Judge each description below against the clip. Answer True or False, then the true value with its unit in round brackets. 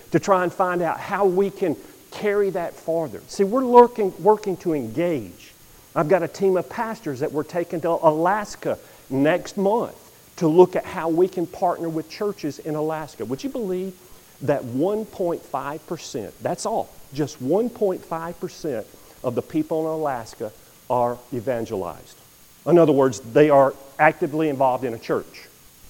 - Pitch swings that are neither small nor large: True (4.1 semitones)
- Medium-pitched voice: True (165 Hz)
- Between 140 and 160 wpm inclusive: True (155 wpm)